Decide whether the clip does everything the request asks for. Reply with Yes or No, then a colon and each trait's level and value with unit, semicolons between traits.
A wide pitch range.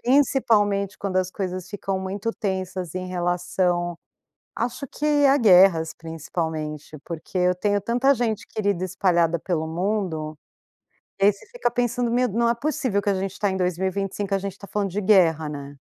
No: average, 3.3 semitones